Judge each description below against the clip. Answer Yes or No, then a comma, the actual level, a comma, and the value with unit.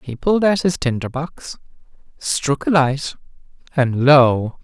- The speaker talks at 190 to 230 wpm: No, average, 140 wpm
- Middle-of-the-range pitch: Yes, medium, 145 Hz